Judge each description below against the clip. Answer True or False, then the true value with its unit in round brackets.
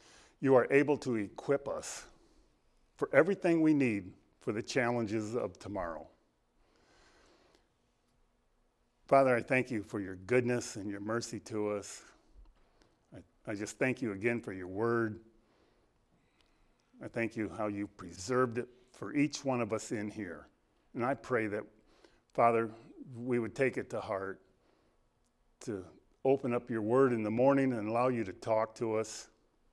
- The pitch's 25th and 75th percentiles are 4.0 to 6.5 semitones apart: False (3.0 semitones)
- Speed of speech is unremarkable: True (155 wpm)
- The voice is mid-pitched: False (115 Hz)